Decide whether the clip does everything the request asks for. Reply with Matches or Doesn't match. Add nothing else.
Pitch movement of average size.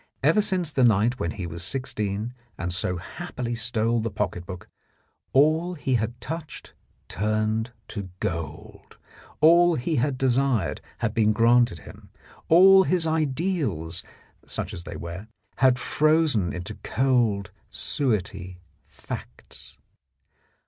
Doesn't match